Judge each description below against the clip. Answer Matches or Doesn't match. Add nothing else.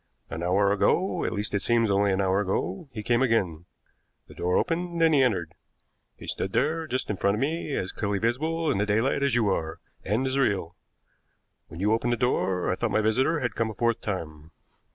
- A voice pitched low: Matches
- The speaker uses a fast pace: Matches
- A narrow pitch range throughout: Doesn't match